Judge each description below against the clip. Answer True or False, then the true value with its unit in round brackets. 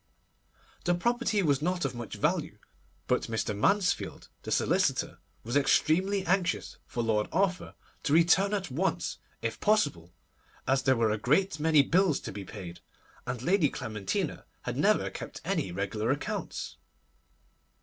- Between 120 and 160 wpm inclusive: True (145 wpm)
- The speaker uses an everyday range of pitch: False (8.8 semitones)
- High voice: False (150 Hz)